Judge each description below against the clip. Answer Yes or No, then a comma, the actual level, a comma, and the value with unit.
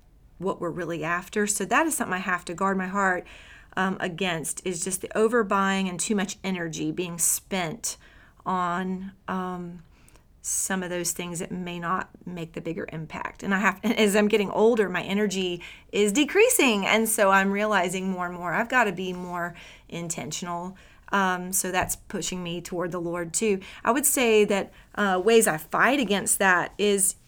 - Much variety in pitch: No, average, 2.8 semitones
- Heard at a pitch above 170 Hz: Yes, medium, 185 Hz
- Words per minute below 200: Yes, average, 185 wpm